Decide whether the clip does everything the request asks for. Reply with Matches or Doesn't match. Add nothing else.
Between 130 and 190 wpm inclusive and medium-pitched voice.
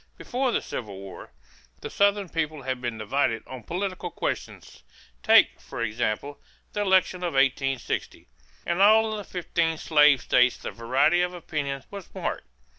Matches